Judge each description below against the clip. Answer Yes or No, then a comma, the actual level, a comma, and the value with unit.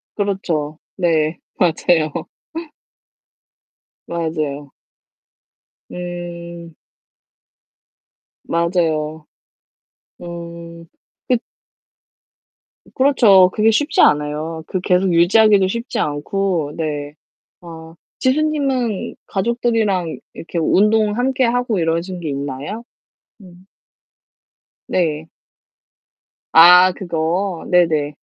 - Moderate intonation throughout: Yes, average, 4.0 semitones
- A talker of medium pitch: Yes, medium, 175 Hz